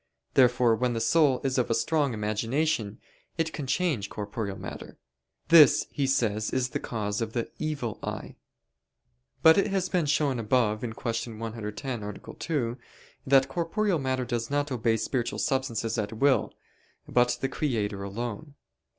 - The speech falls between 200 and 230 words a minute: No, average, 150 wpm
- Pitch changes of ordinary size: Yes, average, 4.3 semitones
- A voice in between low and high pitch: No, low, 125 Hz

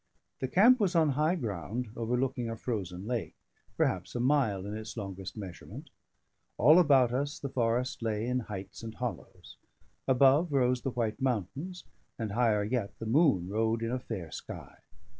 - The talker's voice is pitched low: Yes, low, 120 Hz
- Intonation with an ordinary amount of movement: Yes, average, 4.0 semitones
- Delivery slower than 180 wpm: Yes, average, 165 wpm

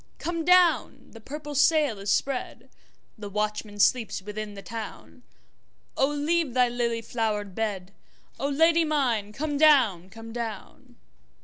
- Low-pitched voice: No, high, 235 Hz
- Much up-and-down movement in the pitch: Yes, wide, 5.8 semitones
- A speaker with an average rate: No, slow, 120 wpm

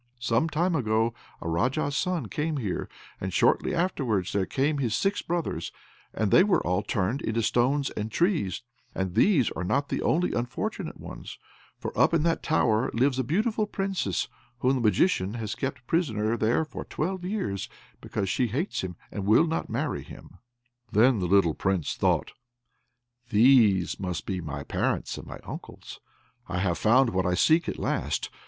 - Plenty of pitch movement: Yes, wide, 8.1 semitones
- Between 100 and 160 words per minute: No, average, 170 wpm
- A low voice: Yes, low, 120 Hz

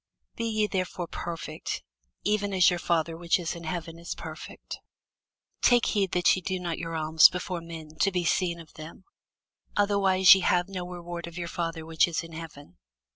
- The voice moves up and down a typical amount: No, narrow, 2.1 semitones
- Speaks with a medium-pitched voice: Yes, medium, 175 Hz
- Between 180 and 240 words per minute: Yes, average, 185 wpm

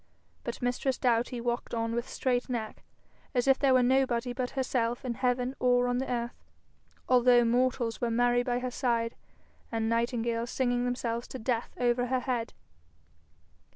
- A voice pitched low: No, high, 245 Hz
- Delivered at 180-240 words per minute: No, average, 160 wpm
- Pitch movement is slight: Yes, narrow, 1.2 semitones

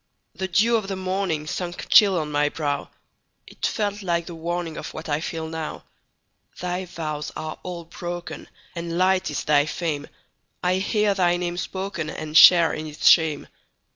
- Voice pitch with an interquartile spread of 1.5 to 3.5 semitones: Yes, average, 2.9 semitones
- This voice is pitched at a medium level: Yes, medium, 170 Hz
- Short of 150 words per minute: Yes, average, 140 wpm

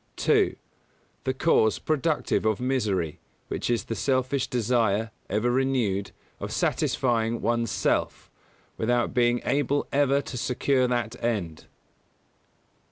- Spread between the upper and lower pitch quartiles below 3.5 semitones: Yes, average, 3.0 semitones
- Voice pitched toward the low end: Yes, low, 120 Hz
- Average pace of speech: No, slow, 115 wpm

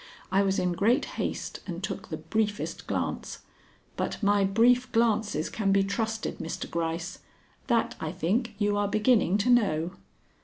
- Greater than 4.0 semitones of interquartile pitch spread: No, average, 3.1 semitones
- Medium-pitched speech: No, high, 205 Hz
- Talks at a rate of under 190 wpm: Yes, average, 155 wpm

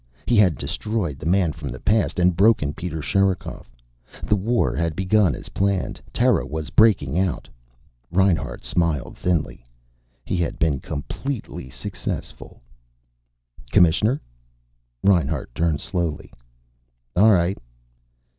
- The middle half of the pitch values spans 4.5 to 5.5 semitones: No, average, 4.0 semitones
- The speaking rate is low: Yes, slow, 115 wpm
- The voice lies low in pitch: Yes, very low, 90 Hz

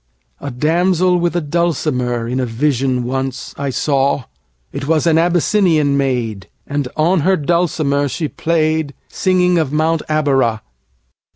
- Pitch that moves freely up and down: No, average, 4.2 semitones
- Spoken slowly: Yes, slow, 115 wpm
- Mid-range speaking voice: Yes, medium, 145 Hz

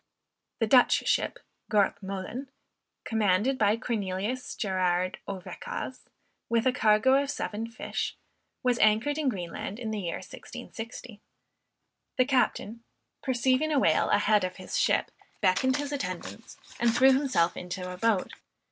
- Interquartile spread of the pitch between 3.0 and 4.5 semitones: No, average, 5.1 semitones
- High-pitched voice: Yes, high, 220 Hz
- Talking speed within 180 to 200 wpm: No, average, 140 wpm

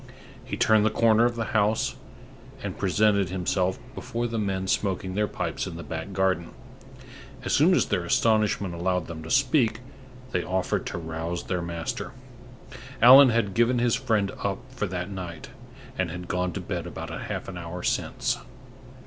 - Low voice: Yes, very low, 95 Hz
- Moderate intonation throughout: Yes, average, 4.0 semitones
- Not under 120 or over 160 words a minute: No, average, 170 wpm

